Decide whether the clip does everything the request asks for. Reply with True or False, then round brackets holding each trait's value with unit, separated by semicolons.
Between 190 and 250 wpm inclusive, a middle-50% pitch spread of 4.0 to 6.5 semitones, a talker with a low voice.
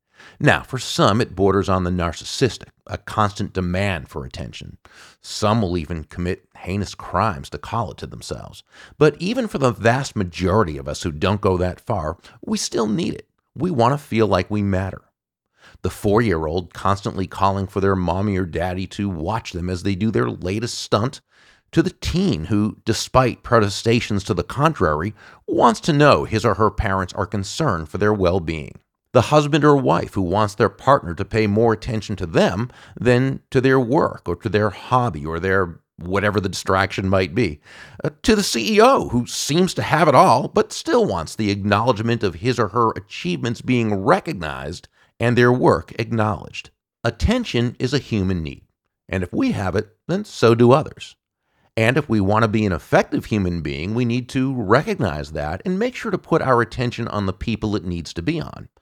True (195 wpm; 4.6 semitones; 105 Hz)